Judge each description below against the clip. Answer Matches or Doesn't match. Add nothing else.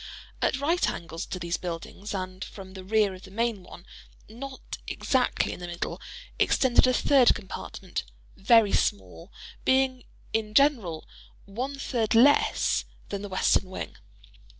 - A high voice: Matches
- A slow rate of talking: Matches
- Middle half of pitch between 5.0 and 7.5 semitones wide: Matches